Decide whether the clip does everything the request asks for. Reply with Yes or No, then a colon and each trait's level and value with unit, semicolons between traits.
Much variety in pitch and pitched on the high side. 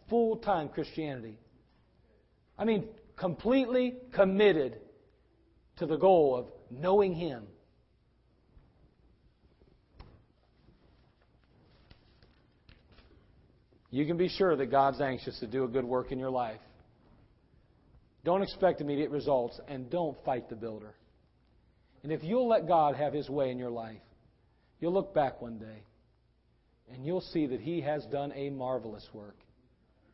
No: wide, 6.5 semitones; medium, 140 Hz